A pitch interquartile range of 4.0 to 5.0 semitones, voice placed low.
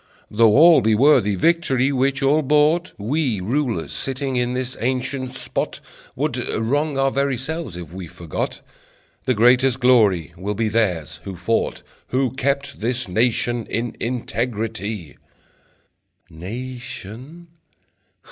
Yes: average, 4.3 semitones; low, 125 Hz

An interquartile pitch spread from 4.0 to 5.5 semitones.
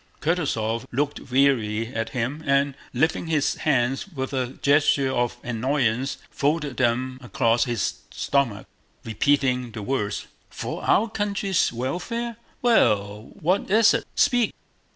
Yes: average, 4.6 semitones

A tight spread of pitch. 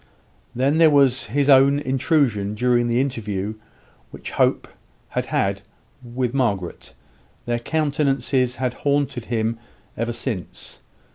No: average, 3.1 semitones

